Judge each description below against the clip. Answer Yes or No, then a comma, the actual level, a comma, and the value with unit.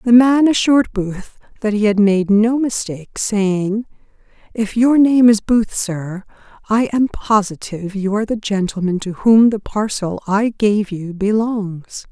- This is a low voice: No, high, 210 Hz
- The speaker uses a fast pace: No, average, 160 wpm